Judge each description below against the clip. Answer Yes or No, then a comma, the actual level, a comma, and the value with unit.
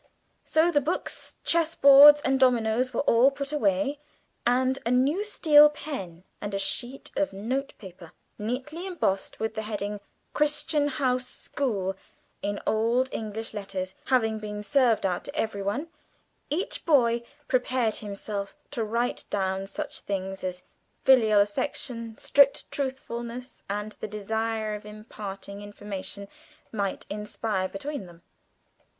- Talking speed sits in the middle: No, slow, 130 wpm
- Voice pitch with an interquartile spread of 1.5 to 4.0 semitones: No, average, 5.1 semitones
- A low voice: No, high, 230 Hz